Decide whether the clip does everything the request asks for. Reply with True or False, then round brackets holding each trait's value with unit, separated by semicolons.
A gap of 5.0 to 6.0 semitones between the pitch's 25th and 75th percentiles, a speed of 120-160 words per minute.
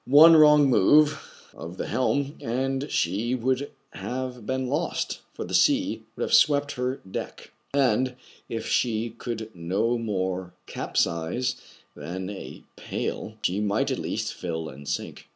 True (5.6 semitones; 145 wpm)